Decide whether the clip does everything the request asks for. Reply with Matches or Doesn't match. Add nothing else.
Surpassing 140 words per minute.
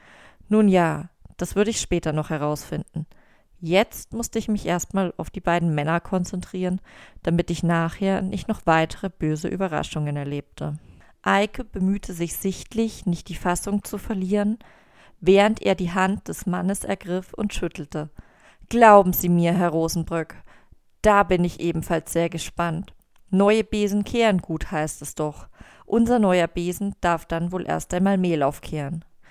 Matches